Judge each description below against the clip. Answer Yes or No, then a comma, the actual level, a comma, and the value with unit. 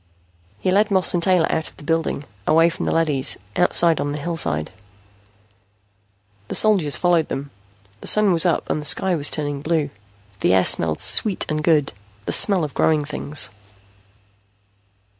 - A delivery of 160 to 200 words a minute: Yes, average, 165 wpm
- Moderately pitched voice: Yes, medium, 160 Hz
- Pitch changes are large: No, average, 3.4 semitones